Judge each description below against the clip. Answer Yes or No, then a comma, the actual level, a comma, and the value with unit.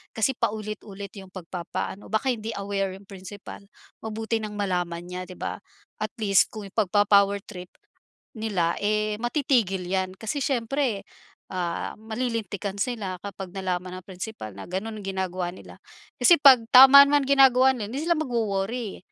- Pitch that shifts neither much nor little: Yes, average, 3.4 semitones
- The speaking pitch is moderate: No, high, 205 Hz